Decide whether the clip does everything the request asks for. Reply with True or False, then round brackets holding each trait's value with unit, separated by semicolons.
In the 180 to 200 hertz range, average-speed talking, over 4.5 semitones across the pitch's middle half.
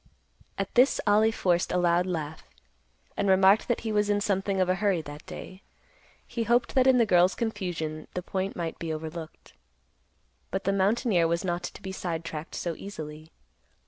False (185 Hz; 175 wpm; 3.5 semitones)